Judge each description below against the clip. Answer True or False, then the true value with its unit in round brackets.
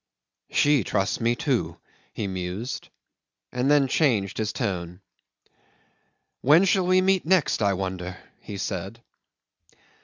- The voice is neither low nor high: False (110 Hz)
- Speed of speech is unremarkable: False (120 wpm)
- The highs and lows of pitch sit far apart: True (7.4 semitones)